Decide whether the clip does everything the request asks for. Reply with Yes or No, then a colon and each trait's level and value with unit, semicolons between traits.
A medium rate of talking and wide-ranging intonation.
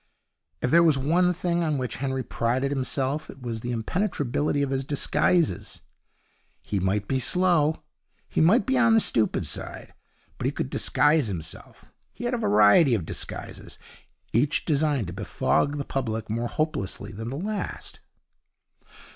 Yes: average, 155 wpm; wide, 5.8 semitones